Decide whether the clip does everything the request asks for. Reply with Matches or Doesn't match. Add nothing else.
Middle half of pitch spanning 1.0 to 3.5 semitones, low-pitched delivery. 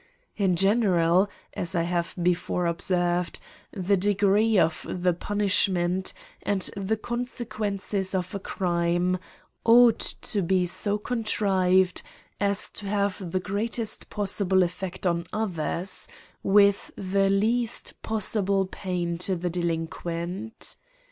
Doesn't match